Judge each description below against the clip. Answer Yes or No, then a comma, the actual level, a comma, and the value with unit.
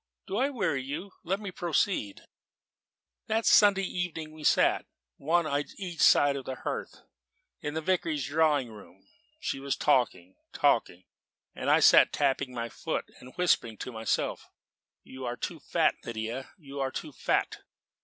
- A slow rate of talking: No, average, 155 wpm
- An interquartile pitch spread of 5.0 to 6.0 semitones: Yes, wide, 5.5 semitones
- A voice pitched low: No, medium, 145 Hz